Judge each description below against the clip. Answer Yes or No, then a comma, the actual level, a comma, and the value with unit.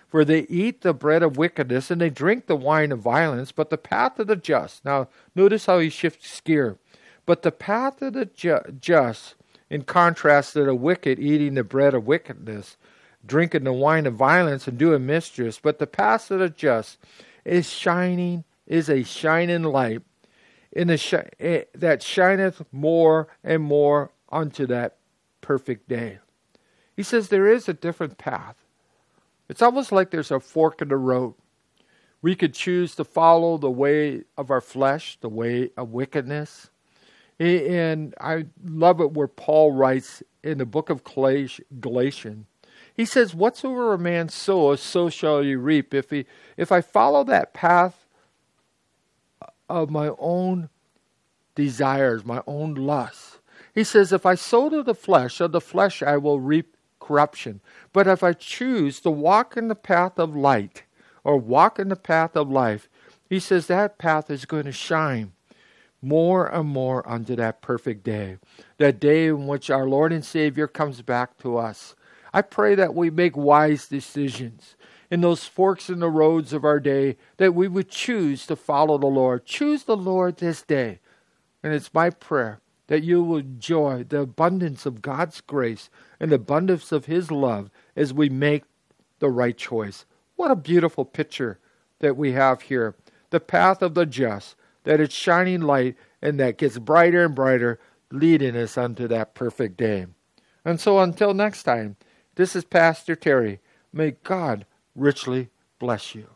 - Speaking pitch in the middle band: Yes, medium, 155 Hz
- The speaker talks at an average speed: Yes, average, 170 wpm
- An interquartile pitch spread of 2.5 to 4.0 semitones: No, average, 4.5 semitones